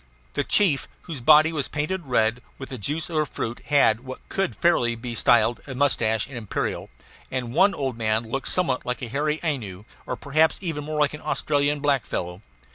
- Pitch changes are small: No, average, 4.4 semitones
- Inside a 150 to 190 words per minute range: No, average, 200 wpm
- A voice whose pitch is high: No, low, 135 Hz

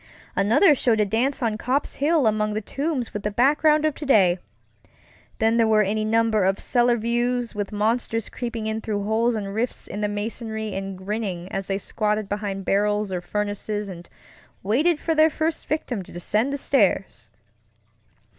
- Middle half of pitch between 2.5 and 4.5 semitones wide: Yes, average, 3.0 semitones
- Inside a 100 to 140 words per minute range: No, average, 175 wpm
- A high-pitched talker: Yes, high, 220 Hz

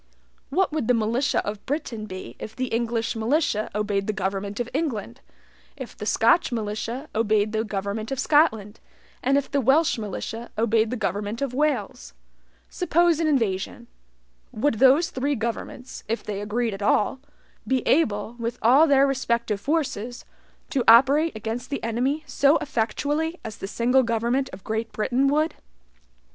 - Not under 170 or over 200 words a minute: No, average, 155 wpm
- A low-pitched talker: No, high, 235 Hz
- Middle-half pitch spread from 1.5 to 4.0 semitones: No, average, 4.4 semitones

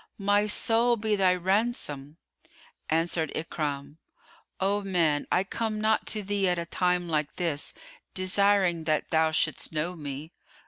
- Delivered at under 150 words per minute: Yes, average, 140 wpm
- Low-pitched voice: No, medium, 180 Hz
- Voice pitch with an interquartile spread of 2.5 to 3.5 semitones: No, average, 4.3 semitones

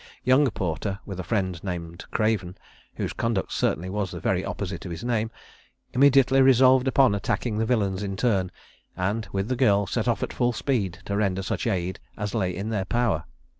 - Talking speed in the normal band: Yes, average, 190 wpm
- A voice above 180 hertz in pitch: No, low, 100 Hz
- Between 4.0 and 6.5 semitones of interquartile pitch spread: Yes, average, 4.3 semitones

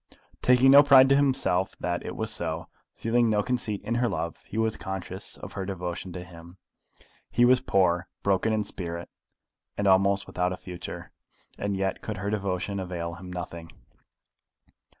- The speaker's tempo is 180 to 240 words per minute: No, average, 170 wpm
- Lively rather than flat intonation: No, average, 3.8 semitones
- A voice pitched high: No, very low, 95 Hz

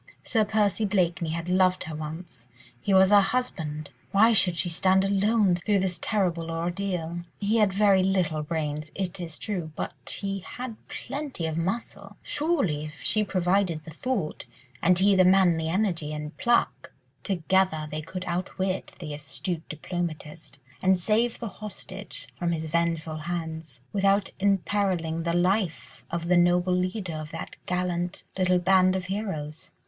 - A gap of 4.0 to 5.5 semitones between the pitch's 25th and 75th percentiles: No, average, 3.3 semitones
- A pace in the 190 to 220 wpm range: No, average, 155 wpm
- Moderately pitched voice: Yes, medium, 180 Hz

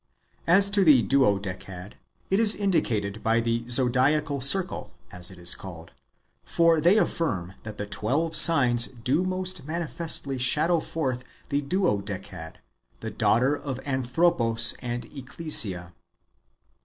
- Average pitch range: No, wide, 7.5 semitones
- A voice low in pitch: Yes, low, 130 Hz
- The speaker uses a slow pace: Yes, slow, 125 wpm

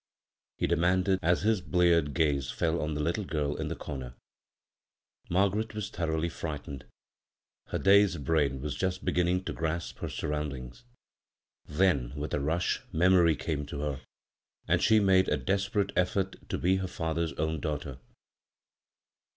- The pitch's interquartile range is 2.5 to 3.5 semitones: No, average, 4.0 semitones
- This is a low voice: Yes, very low, 85 Hz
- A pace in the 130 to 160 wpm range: Yes, average, 150 wpm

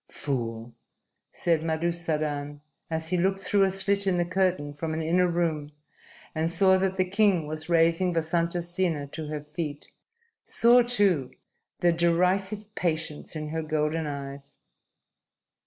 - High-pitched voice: No, medium, 165 Hz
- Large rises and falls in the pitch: No, average, 3.3 semitones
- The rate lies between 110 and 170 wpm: Yes, average, 140 wpm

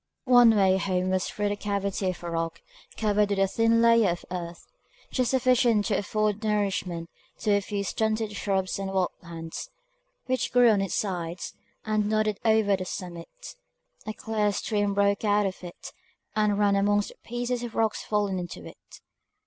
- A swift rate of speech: No, average, 175 wpm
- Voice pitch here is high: Yes, high, 205 Hz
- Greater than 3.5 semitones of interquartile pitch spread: No, narrow, 2.5 semitones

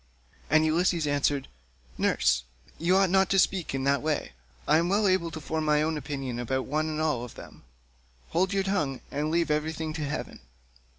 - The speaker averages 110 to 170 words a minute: No, average, 190 wpm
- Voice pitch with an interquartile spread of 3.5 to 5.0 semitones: No, average, 3.0 semitones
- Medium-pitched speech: Yes, medium, 155 Hz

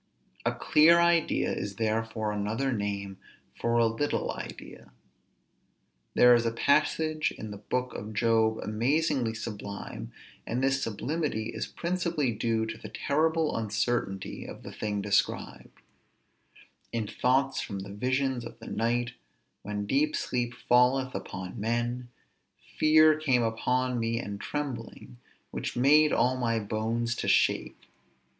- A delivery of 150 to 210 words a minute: No, slow, 135 wpm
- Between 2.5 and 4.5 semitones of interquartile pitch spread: Yes, average, 3.7 semitones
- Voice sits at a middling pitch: No, low, 120 Hz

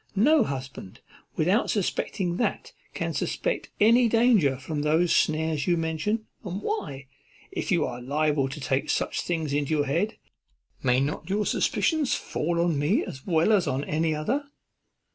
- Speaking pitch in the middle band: Yes, medium, 160 Hz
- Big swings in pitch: Yes, wide, 6.4 semitones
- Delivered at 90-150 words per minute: No, average, 160 wpm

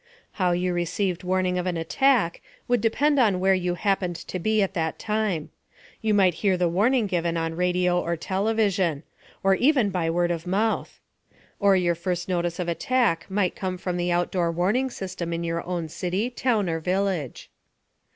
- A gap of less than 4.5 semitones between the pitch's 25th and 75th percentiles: Yes, average, 2.8 semitones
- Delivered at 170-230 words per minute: Yes, average, 180 wpm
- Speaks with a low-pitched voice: No, medium, 180 Hz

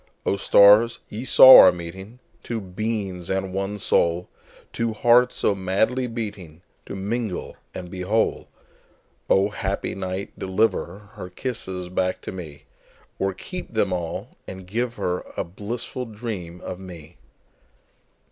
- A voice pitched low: Yes, very low, 95 Hz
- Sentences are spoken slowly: Yes, slow, 115 wpm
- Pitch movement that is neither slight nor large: Yes, average, 3.6 semitones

